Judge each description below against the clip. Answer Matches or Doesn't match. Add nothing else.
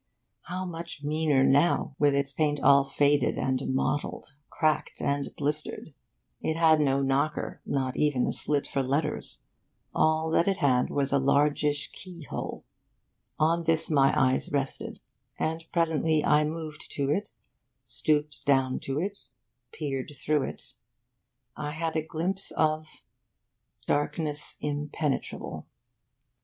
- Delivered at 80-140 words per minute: Matches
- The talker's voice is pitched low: Doesn't match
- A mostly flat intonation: Matches